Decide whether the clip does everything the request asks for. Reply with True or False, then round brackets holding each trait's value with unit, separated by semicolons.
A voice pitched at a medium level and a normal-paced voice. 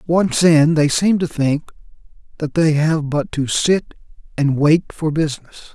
True (155 Hz; 165 wpm)